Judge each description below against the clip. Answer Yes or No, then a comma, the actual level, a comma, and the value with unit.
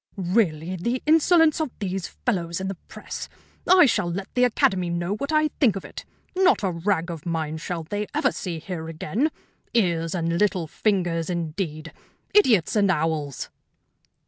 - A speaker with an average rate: Yes, average, 165 wpm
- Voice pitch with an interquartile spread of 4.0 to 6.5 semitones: Yes, average, 4.9 semitones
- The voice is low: No, medium, 185 Hz